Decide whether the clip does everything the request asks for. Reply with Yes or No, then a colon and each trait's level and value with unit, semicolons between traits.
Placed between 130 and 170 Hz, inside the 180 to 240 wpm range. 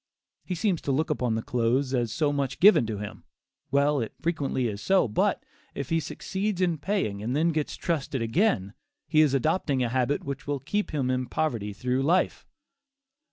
Yes: medium, 140 Hz; average, 190 wpm